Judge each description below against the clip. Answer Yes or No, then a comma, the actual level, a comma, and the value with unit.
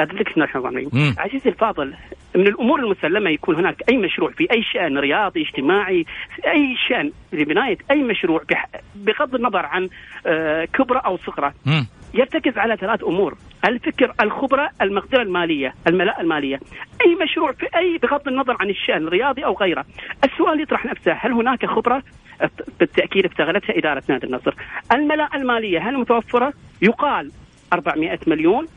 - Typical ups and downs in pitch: No, wide, 8.4 semitones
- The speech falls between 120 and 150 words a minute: Yes, slow, 135 wpm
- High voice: Yes, high, 235 Hz